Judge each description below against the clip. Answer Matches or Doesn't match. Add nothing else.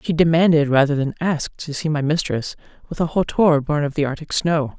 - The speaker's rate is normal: Doesn't match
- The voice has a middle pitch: Matches